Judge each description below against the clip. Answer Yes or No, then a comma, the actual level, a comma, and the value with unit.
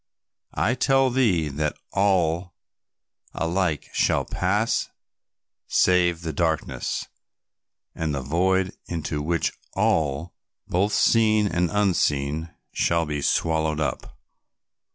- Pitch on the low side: Yes, very low, 85 Hz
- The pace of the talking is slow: Yes, slow, 100 wpm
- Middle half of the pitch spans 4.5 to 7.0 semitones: No, average, 3.5 semitones